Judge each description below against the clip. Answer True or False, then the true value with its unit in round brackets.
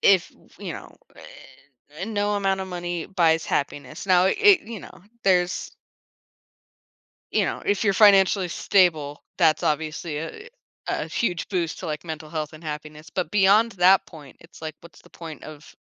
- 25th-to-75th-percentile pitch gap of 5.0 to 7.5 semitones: False (3.9 semitones)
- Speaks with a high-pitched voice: False (175 Hz)